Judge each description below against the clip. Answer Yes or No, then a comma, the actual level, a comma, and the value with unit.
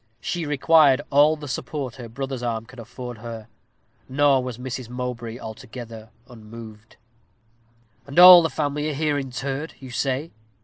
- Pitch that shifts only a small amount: No, average, 3.8 semitones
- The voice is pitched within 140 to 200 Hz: No, low, 130 Hz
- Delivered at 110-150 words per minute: Yes, average, 145 wpm